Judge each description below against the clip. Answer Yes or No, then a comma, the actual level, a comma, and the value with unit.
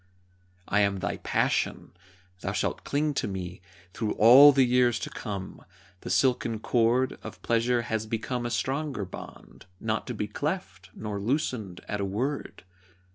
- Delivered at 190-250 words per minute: No, average, 155 wpm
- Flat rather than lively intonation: No, average, 4.0 semitones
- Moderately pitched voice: No, low, 115 Hz